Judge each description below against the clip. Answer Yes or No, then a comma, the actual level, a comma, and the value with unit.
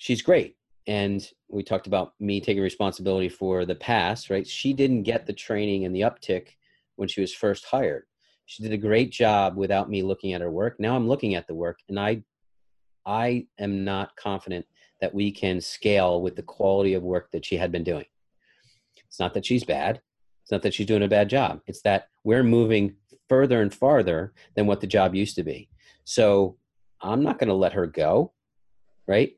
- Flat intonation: Yes, narrow, 2.1 semitones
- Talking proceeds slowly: No, average, 200 wpm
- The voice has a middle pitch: No, low, 100 Hz